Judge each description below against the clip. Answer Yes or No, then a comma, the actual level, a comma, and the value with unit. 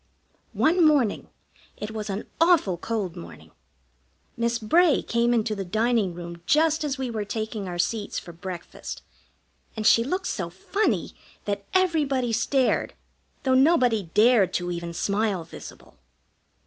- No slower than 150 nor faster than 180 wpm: No, average, 140 wpm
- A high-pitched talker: Yes, high, 220 Hz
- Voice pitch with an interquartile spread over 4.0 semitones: Yes, wide, 5.6 semitones